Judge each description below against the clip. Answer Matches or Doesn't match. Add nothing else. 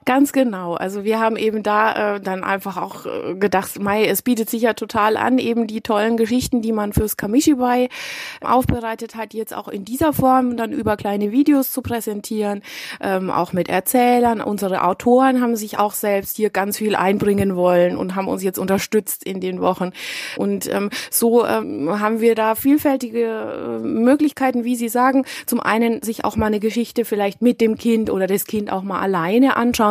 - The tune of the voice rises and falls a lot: Doesn't match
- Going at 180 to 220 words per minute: Matches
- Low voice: Doesn't match